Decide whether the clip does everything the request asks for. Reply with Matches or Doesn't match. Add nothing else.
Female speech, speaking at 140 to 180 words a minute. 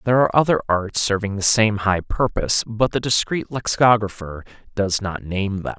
Doesn't match